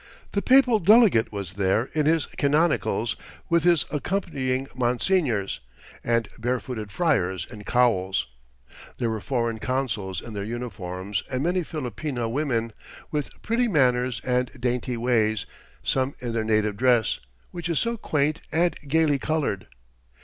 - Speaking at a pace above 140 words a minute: No, slow, 135 wpm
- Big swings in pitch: Yes, wide, 5.8 semitones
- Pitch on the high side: No, low, 125 Hz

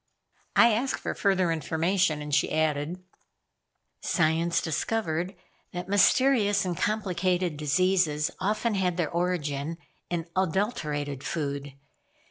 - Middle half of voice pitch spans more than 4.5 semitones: No, average, 3.9 semitones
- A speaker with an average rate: No, slow, 105 wpm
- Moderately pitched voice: Yes, medium, 175 Hz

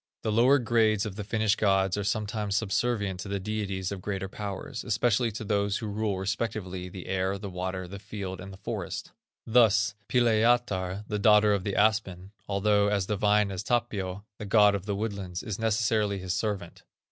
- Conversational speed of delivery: Yes, average, 180 wpm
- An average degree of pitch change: No, narrow, 2.1 semitones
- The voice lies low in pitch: Yes, low, 105 Hz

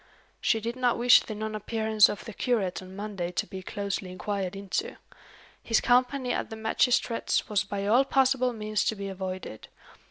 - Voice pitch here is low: No, high, 215 Hz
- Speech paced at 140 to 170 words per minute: No, average, 180 wpm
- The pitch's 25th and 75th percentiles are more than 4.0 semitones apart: No, average, 3.6 semitones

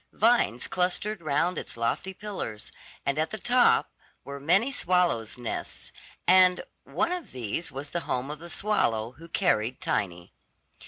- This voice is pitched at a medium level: Yes, medium, 165 Hz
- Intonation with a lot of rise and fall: Yes, wide, 7.4 semitones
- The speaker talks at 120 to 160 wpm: Yes, average, 150 wpm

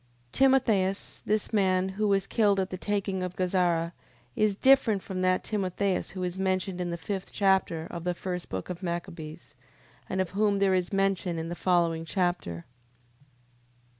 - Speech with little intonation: Yes, narrow, 2.0 semitones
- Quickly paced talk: No, average, 165 wpm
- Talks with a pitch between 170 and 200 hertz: Yes, medium, 185 Hz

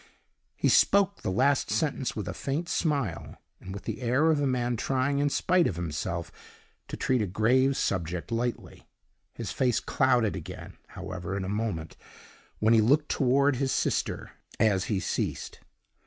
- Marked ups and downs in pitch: Yes, wide, 6.2 semitones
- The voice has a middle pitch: No, low, 120 Hz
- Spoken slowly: No, average, 165 wpm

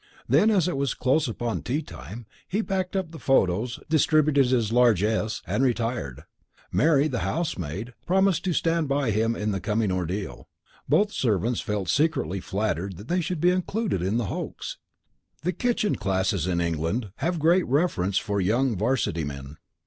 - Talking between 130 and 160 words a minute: No, average, 170 wpm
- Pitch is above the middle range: No, low, 120 Hz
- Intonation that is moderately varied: No, wide, 8.5 semitones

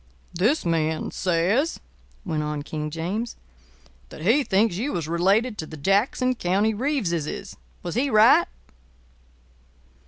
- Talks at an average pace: No, slow, 125 wpm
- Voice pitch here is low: No, high, 190 Hz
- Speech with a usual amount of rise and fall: No, wide, 6.0 semitones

